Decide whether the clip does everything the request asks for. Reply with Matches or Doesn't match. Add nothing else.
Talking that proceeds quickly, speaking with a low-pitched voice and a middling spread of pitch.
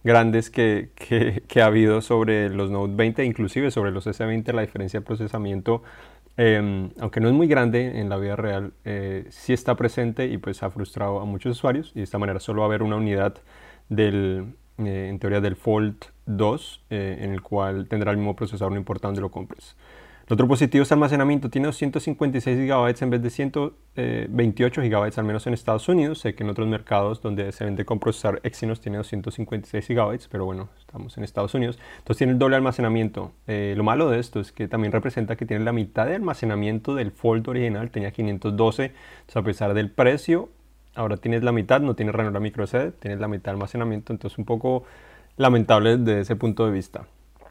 Matches